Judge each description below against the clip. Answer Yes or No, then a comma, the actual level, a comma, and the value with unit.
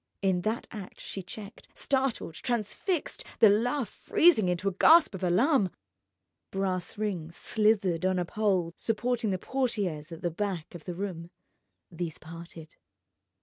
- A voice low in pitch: No, high, 195 Hz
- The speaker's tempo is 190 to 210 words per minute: No, average, 145 wpm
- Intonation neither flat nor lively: Yes, average, 4.3 semitones